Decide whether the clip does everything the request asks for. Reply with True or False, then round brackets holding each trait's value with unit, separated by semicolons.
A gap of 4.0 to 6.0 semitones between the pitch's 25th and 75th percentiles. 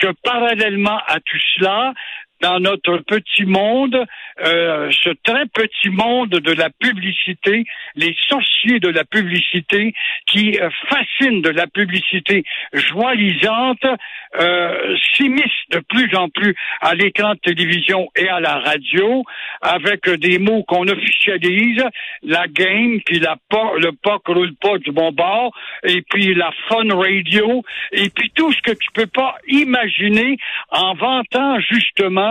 True (4.6 semitones)